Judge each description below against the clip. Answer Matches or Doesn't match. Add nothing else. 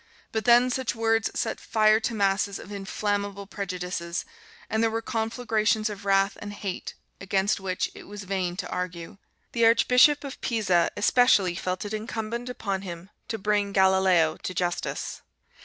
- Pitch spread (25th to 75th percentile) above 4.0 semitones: Doesn't match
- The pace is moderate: Matches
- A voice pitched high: Matches